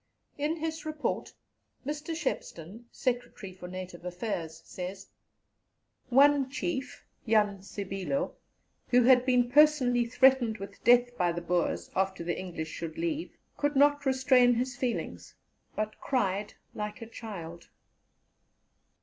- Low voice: No, high, 240 Hz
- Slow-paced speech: Yes, slow, 125 wpm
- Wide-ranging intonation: Yes, wide, 6.2 semitones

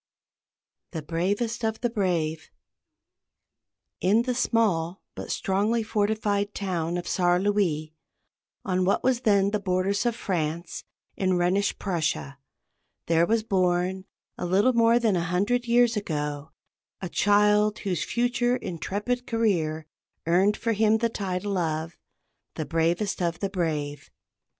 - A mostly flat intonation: No, average, 4.2 semitones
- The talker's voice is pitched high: Yes, high, 195 Hz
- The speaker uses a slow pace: Yes, slow, 130 wpm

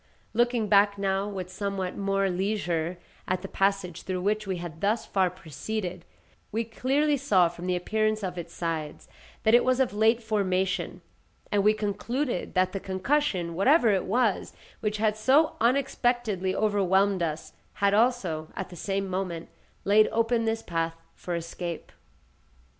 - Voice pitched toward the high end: Yes, high, 200 Hz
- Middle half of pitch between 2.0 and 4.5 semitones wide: Yes, average, 3.3 semitones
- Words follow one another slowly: No, average, 155 wpm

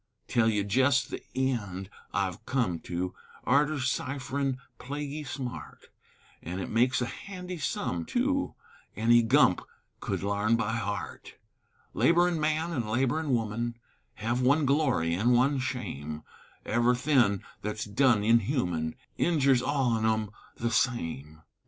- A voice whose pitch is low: Yes, low, 120 Hz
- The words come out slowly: Yes, slow, 130 wpm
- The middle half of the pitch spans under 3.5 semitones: No, average, 5.1 semitones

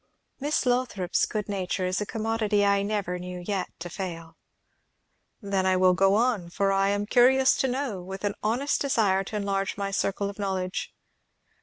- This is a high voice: Yes, high, 200 Hz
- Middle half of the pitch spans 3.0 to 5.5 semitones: No, narrow, 2.6 semitones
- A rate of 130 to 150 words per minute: No, average, 175 wpm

